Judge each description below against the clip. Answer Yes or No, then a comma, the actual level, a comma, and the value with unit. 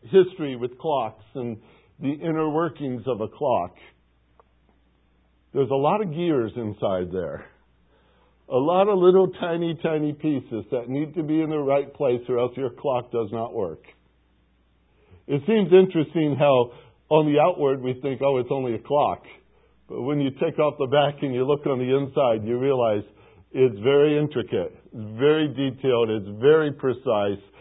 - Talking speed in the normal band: Yes, average, 165 wpm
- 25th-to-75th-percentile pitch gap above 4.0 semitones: Yes, wide, 5.4 semitones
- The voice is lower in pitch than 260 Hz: Yes, low, 135 Hz